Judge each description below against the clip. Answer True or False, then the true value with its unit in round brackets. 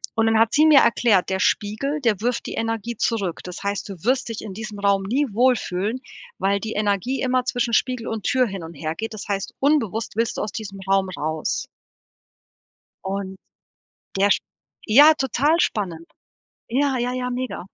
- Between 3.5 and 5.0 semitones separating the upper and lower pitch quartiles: True (4.2 semitones)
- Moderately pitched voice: False (220 Hz)